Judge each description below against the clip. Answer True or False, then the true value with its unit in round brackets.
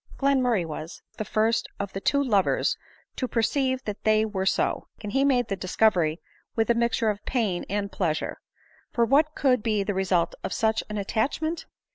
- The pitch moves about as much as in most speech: True (4.3 semitones)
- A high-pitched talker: True (220 Hz)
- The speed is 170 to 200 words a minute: True (180 wpm)